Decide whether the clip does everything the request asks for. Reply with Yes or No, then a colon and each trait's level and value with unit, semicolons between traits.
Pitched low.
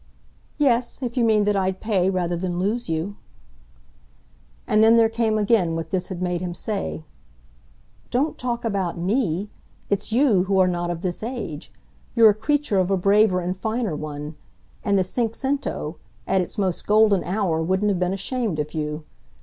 No: high, 195 Hz